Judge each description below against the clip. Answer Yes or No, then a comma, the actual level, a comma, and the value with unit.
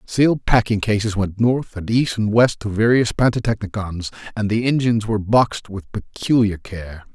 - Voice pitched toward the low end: Yes, low, 110 Hz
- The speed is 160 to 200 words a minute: Yes, average, 170 wpm